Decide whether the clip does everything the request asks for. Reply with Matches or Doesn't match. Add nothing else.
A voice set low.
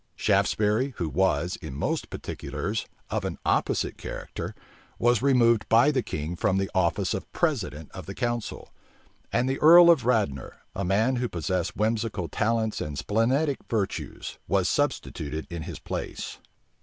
Matches